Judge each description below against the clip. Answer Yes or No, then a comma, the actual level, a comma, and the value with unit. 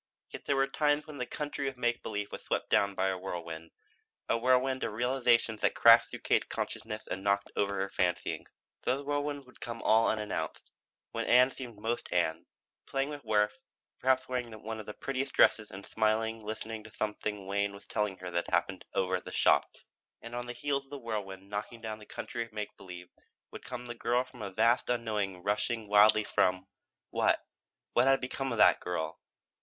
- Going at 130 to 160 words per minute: No, average, 200 wpm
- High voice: No, low, 110 Hz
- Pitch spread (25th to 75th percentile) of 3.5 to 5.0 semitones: Yes, average, 3.9 semitones